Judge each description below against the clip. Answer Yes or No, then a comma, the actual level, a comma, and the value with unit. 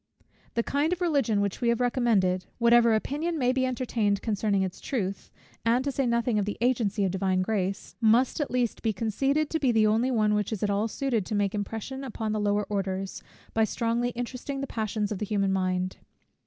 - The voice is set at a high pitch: Yes, high, 225 Hz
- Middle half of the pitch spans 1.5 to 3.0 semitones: No, average, 3.6 semitones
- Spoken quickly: Yes, fast, 210 wpm